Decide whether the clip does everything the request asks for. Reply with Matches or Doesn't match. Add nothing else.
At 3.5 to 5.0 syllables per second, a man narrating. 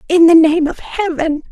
Doesn't match